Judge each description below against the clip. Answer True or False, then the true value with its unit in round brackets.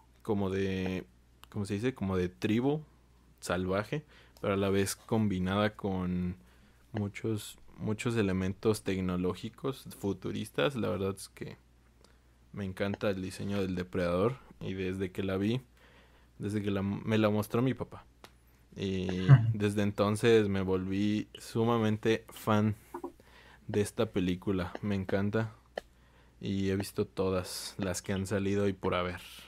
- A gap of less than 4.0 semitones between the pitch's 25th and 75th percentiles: True (2.7 semitones)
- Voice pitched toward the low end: True (100 Hz)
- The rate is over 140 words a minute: False (135 wpm)